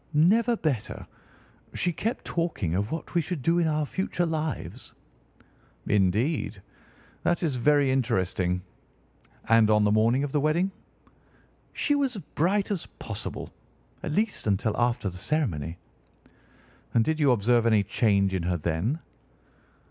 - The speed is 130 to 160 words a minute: Yes, average, 140 wpm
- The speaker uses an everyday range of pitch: No, wide, 8.2 semitones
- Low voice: Yes, low, 130 Hz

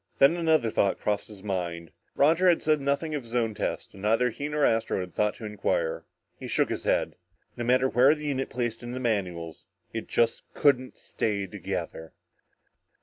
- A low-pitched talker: Yes, low, 120 Hz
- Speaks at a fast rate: No, average, 185 wpm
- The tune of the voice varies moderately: No, wide, 5.7 semitones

